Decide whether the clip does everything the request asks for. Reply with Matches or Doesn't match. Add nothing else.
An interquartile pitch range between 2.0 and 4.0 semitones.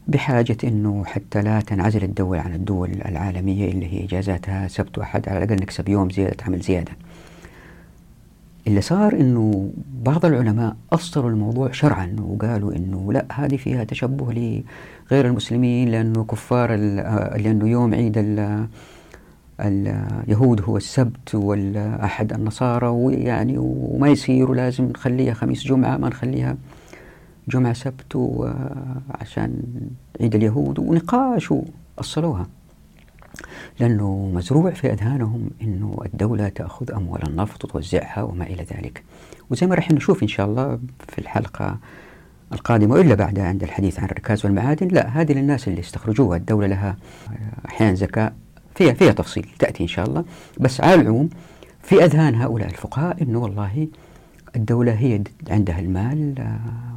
Doesn't match